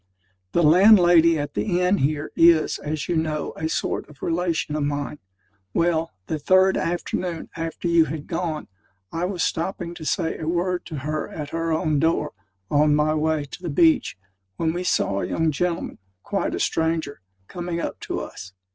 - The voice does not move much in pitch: Yes, narrow, 2.2 semitones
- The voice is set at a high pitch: No, medium, 165 Hz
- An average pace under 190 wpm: Yes, average, 180 wpm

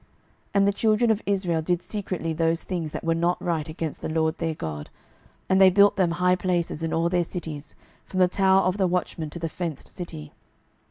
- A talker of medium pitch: Yes, medium, 175 Hz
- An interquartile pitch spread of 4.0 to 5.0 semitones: No, narrow, 2.5 semitones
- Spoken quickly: Yes, fast, 215 wpm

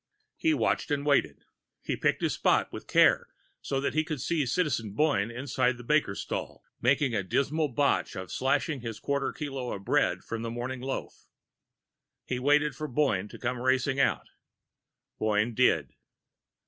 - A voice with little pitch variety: No, average, 3.7 semitones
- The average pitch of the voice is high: No, low, 130 Hz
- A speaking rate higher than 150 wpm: Yes, average, 165 wpm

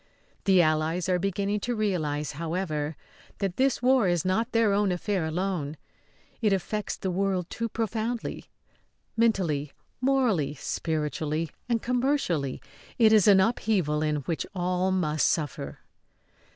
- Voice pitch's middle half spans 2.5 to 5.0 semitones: No, wide, 5.6 semitones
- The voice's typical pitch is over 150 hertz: Yes, medium, 185 Hz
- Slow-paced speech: Yes, slow, 130 wpm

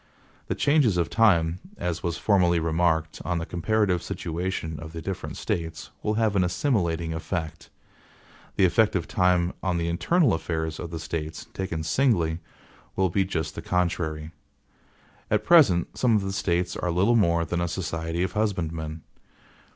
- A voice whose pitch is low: Yes, very low, 85 Hz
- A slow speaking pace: No, average, 160 wpm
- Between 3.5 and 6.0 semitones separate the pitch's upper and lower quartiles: No, average, 3.0 semitones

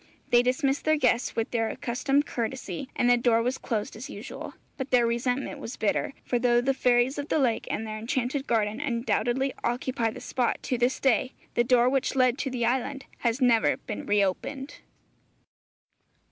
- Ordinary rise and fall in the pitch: No, narrow, 2.3 semitones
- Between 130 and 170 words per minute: No, average, 180 wpm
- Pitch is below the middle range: No, high, 245 Hz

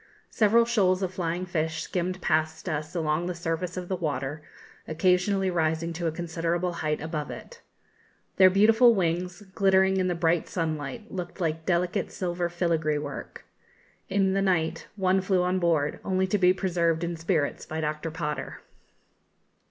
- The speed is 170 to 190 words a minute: No, average, 160 wpm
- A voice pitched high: No, medium, 175 Hz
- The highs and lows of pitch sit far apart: No, narrow, 2.6 semitones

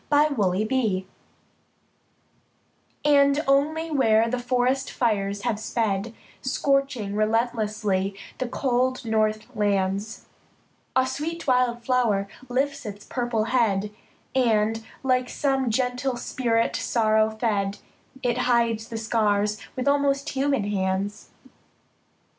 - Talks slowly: Yes, slow, 105 wpm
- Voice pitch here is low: No, high, 230 Hz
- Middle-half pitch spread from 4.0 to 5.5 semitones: No, average, 3.6 semitones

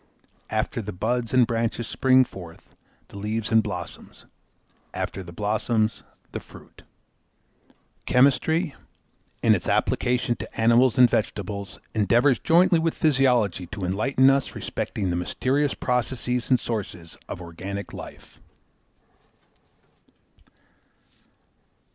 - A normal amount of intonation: Yes, average, 4.3 semitones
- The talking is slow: Yes, slow, 110 wpm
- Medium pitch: No, low, 115 Hz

